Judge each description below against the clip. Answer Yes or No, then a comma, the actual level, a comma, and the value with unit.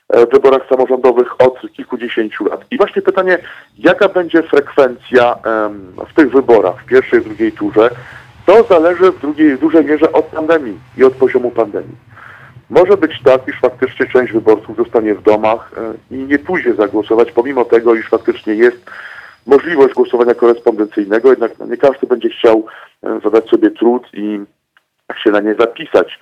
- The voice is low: No, medium, 150 Hz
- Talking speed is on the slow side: No, average, 155 wpm